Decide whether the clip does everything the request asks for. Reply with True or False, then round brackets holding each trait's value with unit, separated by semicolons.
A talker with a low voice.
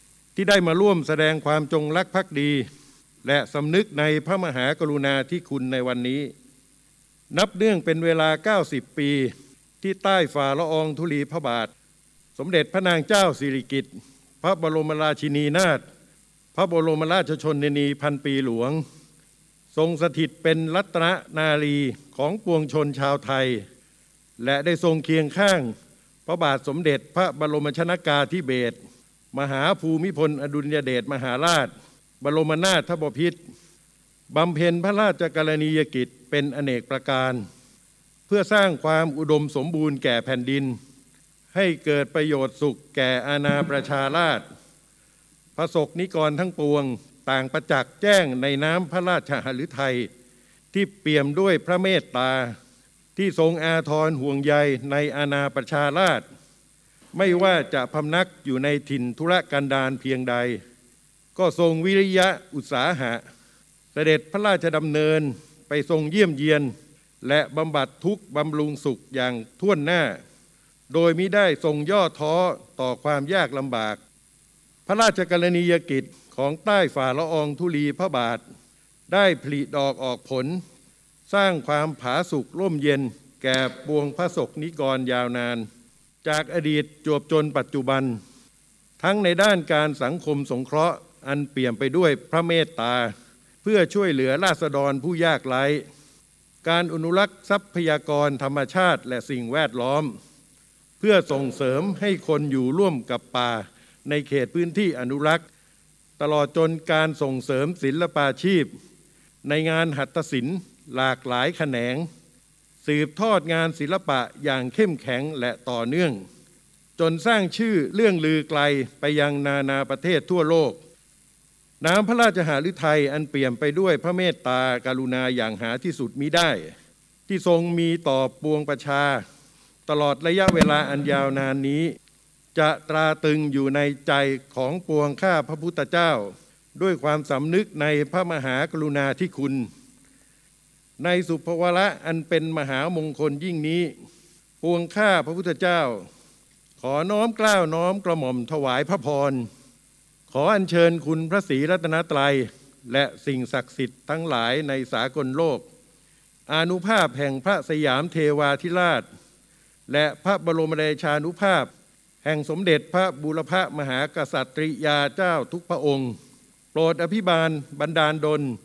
False (150 Hz)